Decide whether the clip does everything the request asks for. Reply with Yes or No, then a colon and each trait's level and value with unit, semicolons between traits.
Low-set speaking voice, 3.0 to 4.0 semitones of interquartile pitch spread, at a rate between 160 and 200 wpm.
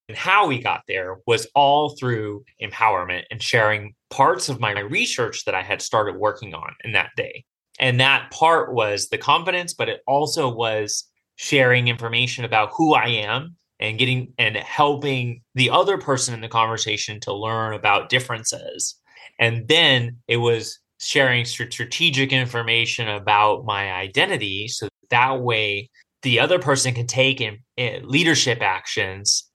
No: low, 120 Hz; average, 3.6 semitones; average, 150 wpm